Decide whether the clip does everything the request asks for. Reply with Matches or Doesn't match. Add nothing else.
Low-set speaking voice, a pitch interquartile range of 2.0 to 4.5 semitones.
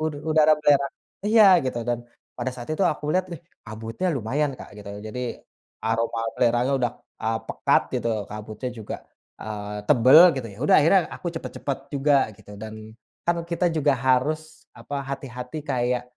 Doesn't match